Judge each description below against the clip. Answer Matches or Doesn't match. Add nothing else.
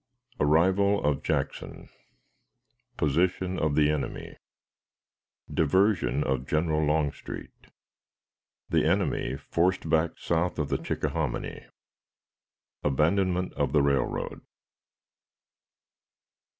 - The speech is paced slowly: Matches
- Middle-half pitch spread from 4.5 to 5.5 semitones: Doesn't match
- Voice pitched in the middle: Doesn't match